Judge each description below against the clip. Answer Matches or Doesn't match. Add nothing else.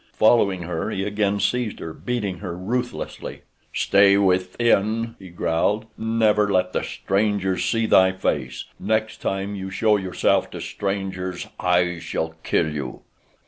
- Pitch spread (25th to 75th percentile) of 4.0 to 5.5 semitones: Doesn't match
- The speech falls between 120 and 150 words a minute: Matches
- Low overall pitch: Matches